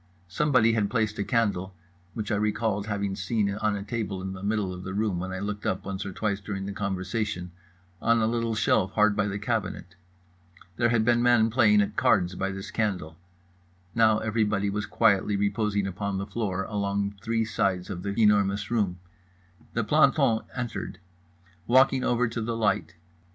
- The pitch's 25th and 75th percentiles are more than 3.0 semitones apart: No, narrow, 2.5 semitones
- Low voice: Yes, low, 105 Hz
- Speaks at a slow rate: No, average, 175 wpm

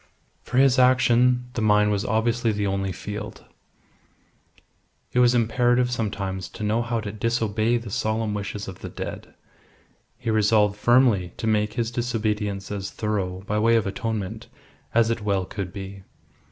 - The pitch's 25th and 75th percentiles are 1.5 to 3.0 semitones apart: Yes, narrow, 2.5 semitones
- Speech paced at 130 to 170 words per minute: Yes, average, 155 wpm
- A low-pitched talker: Yes, low, 110 Hz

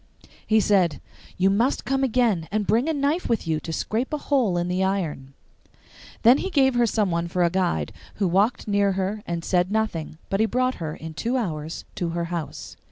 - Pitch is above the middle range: Yes, high, 195 Hz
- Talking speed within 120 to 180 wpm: No, fast, 205 wpm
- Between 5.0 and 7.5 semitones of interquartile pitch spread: Yes, wide, 5.6 semitones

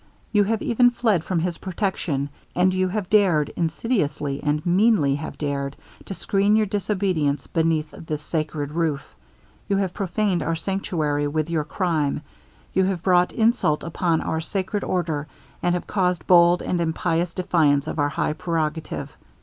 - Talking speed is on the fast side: No, average, 160 wpm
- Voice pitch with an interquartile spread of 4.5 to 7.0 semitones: No, average, 3.9 semitones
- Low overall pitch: No, medium, 170 Hz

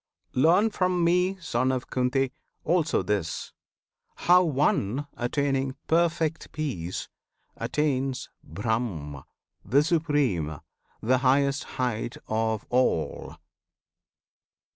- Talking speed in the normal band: No, slow, 90 wpm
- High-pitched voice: No, low, 135 Hz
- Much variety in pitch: Yes, wide, 5.9 semitones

